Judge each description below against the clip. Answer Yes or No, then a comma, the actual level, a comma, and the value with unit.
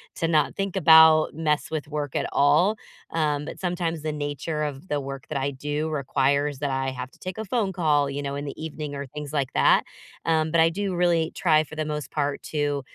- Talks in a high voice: No, medium, 150 Hz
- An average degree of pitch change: No, narrow, 2.2 semitones